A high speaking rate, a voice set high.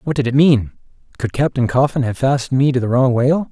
No: fast, 240 wpm; low, 135 Hz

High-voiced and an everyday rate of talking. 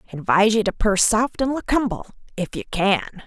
Yes: high, 215 Hz; average, 185 wpm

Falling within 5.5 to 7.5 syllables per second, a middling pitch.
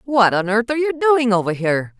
No: 6.0 syllables/s; high, 230 Hz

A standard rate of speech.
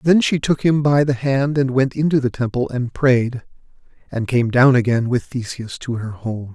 No: fast, 210 wpm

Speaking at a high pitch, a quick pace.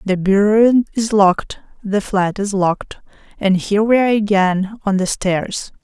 No: high, 200 Hz; average, 165 wpm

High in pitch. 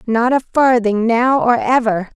Yes: high, 235 Hz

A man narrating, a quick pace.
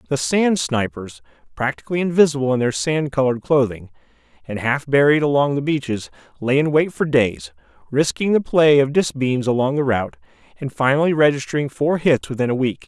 No: male; average, 175 wpm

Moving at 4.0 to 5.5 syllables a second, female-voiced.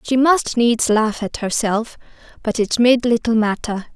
Yes: 4.2 syllables/s; female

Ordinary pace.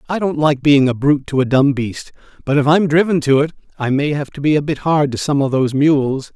No: fast, 275 wpm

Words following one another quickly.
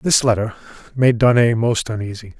No: average, 150 wpm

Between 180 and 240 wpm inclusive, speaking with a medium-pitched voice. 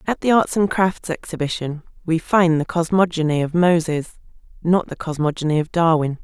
No: average, 165 wpm; medium, 165 Hz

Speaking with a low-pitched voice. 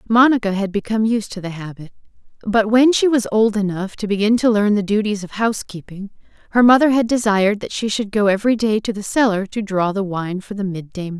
No: high, 210 Hz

